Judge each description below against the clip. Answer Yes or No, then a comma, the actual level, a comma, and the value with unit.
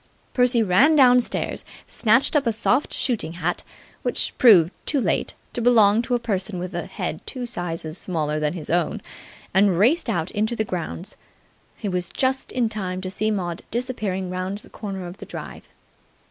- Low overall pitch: No, high, 200 Hz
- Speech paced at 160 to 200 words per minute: Yes, average, 175 wpm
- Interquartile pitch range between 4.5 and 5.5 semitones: Yes, average, 5.1 semitones